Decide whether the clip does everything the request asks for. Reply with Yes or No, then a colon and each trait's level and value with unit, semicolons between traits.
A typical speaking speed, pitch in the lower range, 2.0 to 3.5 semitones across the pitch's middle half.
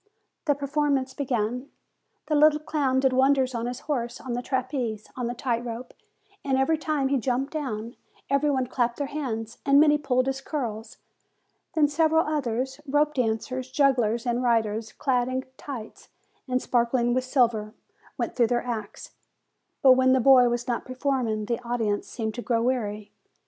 No: average, 170 wpm; very high, 255 Hz; average, 2.7 semitones